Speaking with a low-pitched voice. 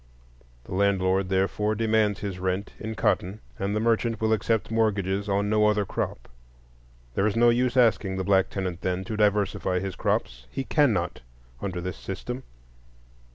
Yes: low, 100 Hz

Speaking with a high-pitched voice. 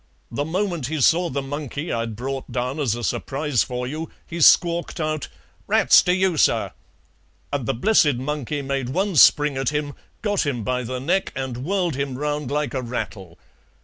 No: medium, 145 Hz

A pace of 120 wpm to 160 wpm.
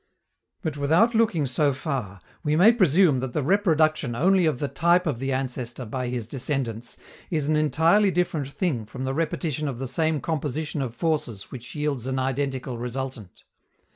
No: average, 170 wpm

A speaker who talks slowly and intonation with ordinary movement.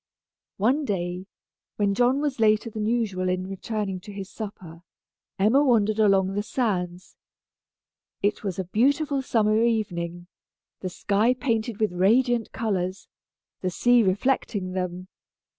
Yes: slow, 130 wpm; average, 4.0 semitones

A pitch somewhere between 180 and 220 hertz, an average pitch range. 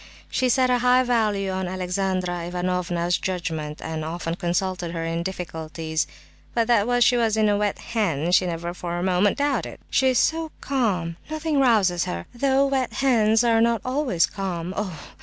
No: high, 190 Hz; wide, 5.7 semitones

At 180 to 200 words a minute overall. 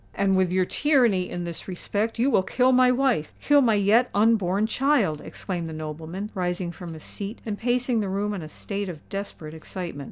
Yes: average, 195 wpm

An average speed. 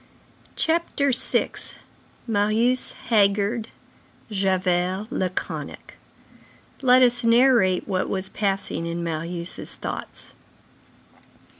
No: slow, 70 wpm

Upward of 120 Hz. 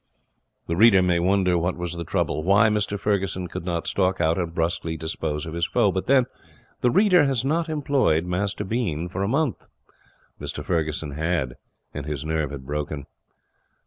No: very low, 90 Hz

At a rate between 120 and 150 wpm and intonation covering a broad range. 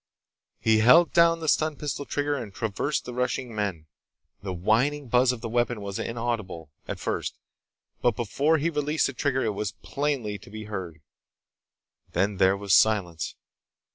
No: average, 165 wpm; wide, 5.9 semitones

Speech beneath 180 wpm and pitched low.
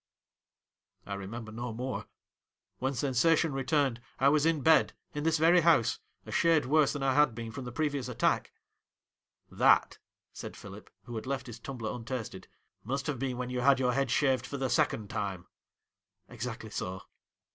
No: average, 190 wpm; low, 130 Hz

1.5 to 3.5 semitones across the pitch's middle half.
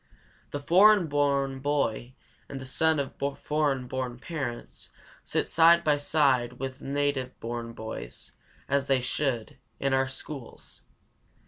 Yes: narrow, 2.4 semitones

